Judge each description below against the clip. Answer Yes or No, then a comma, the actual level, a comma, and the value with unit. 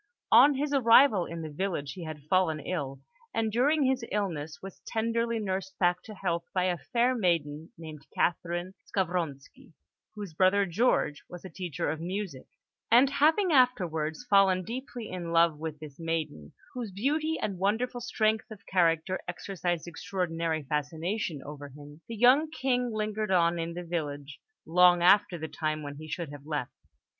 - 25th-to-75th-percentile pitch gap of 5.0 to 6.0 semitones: Yes, wide, 5.4 semitones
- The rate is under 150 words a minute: No, average, 165 wpm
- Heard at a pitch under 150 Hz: No, medium, 180 Hz